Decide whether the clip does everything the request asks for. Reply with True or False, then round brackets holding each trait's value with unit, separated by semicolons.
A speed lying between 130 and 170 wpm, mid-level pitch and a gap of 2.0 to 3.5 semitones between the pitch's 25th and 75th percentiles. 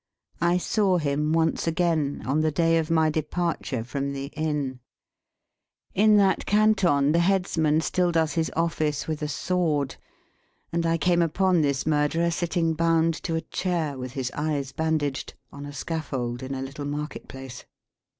True (160 wpm; 155 Hz; 3.0 semitones)